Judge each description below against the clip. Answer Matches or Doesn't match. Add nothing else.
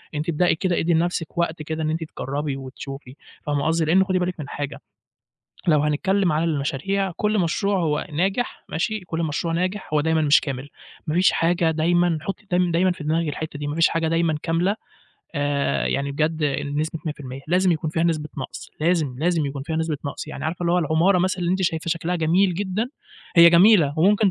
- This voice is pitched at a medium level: Matches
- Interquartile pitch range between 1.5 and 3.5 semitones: Matches